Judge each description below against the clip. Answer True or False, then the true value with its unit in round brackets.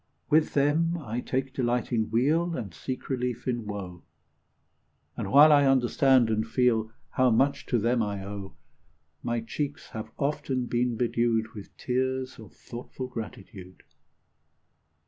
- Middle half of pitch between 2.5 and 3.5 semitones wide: True (3.1 semitones)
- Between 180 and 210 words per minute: False (140 wpm)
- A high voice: False (120 Hz)